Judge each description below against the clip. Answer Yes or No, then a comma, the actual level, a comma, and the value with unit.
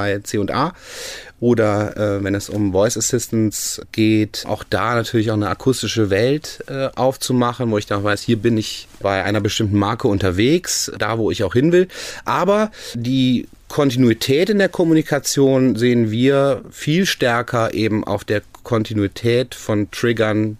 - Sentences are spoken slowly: No, average, 155 wpm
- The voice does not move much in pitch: No, average, 3.5 semitones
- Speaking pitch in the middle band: No, low, 115 Hz